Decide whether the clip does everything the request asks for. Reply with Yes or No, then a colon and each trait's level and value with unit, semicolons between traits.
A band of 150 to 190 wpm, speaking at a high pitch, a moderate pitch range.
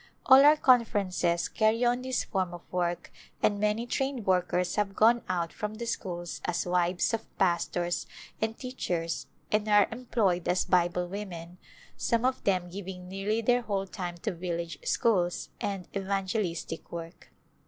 Yes: average, 160 wpm; high, 195 Hz; average, 4.1 semitones